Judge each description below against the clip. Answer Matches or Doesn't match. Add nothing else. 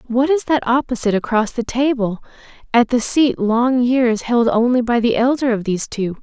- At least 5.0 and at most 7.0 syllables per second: Matches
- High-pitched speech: Matches